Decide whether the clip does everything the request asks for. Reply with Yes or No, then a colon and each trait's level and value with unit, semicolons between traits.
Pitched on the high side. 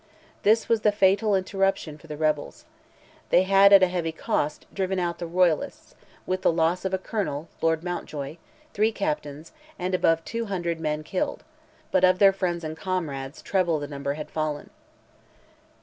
No: medium, 175 Hz